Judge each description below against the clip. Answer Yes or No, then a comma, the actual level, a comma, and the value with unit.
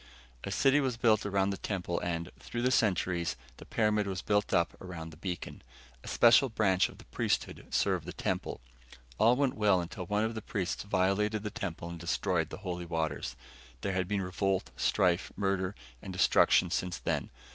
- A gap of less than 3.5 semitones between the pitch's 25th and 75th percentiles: Yes, average, 3.1 semitones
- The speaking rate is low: No, average, 185 wpm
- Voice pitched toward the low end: Yes, very low, 95 Hz